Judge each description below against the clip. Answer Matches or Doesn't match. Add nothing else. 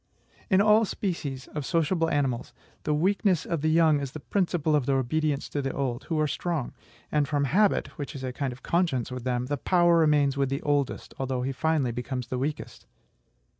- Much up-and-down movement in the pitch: Doesn't match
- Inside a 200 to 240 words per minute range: Matches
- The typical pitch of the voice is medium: Matches